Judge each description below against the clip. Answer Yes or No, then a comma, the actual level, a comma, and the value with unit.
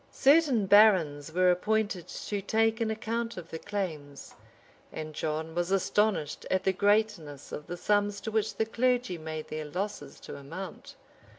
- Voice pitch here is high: Yes, high, 195 Hz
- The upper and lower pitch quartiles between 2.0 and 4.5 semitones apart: No, wide, 5.5 semitones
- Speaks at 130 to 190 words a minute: Yes, average, 160 wpm